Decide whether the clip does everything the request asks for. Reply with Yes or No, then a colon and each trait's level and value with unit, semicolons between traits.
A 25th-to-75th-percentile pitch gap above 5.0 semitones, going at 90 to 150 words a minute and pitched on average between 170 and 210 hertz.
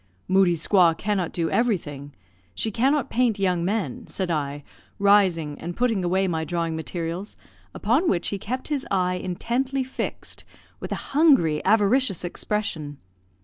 Yes: wide, 5.4 semitones; average, 145 wpm; high, 190 Hz